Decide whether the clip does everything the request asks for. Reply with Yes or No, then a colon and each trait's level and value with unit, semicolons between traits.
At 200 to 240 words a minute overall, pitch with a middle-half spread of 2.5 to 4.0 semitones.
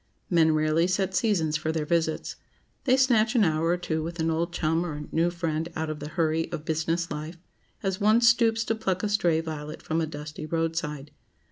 Yes: fast, 205 wpm; average, 2.9 semitones